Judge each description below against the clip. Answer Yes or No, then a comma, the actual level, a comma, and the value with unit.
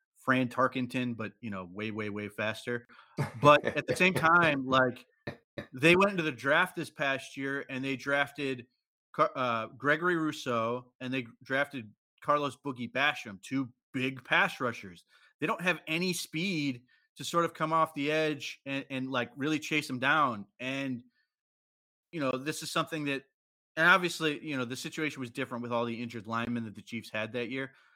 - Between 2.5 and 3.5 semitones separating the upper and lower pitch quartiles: No, average, 4.0 semitones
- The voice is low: Yes, low, 130 Hz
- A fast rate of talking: No, average, 180 wpm